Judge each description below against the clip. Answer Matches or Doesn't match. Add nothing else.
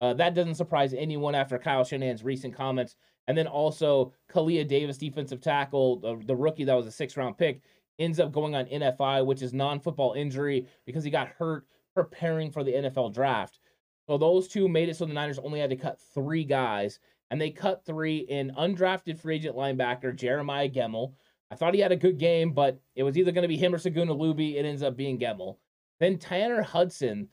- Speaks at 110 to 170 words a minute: Doesn't match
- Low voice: Doesn't match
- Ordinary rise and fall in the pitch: Matches